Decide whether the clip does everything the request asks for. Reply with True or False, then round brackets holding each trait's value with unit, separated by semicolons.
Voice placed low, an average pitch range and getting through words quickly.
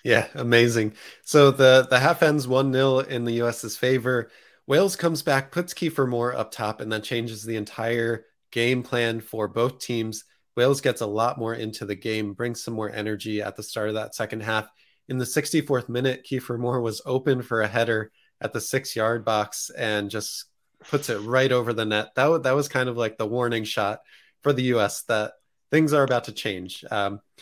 True (120 Hz; 3.0 semitones; 210 wpm)